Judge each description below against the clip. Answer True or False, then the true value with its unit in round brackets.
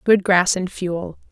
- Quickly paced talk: False (185 wpm)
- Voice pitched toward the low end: False (185 Hz)